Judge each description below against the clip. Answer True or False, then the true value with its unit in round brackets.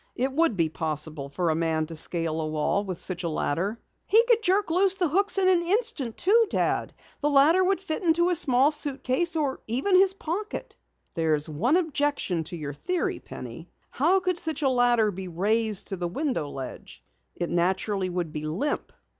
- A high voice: True (250 Hz)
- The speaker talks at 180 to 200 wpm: True (190 wpm)